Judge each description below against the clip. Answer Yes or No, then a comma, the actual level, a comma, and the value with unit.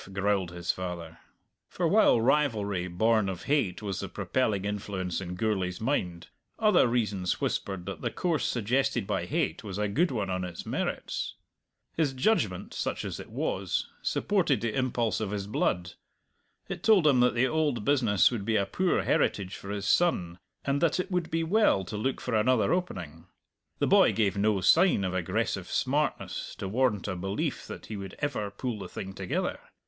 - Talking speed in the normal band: Yes, average, 180 wpm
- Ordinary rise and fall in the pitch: No, wide, 5.8 semitones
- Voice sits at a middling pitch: No, low, 105 Hz